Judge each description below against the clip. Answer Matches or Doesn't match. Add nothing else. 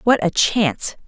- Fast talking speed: Doesn't match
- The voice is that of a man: Doesn't match